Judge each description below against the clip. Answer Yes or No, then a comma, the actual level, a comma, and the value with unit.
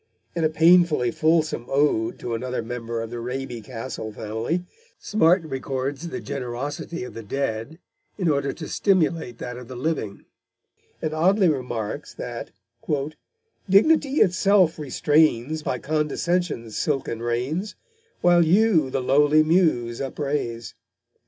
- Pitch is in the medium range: Yes, medium, 145 Hz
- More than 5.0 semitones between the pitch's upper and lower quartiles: Yes, wide, 5.4 semitones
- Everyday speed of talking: No, slow, 125 wpm